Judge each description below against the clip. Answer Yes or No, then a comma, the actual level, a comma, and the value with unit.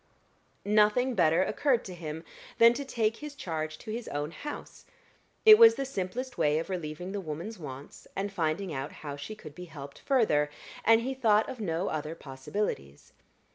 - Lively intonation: Yes, wide, 7.0 semitones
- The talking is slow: No, average, 175 wpm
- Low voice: No, medium, 185 Hz